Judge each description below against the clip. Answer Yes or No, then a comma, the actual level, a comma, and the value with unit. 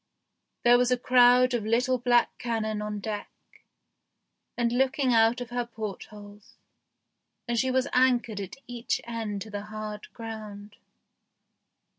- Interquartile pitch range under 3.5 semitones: Yes, narrow, 2.6 semitones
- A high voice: Yes, high, 230 Hz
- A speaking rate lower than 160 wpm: Yes, average, 140 wpm